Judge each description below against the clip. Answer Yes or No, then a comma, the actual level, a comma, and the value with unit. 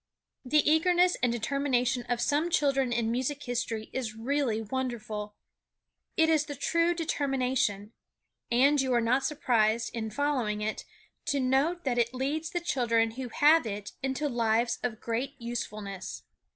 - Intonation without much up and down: No, average, 4.0 semitones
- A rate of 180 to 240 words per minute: No, average, 150 wpm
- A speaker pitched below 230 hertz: No, very high, 255 Hz